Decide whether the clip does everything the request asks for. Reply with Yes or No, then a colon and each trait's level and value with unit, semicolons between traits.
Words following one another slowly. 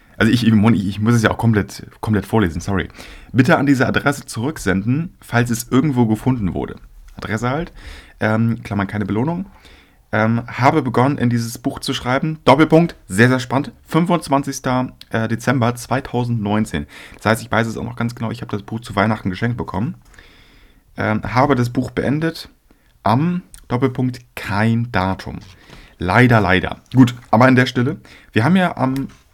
No: average, 165 wpm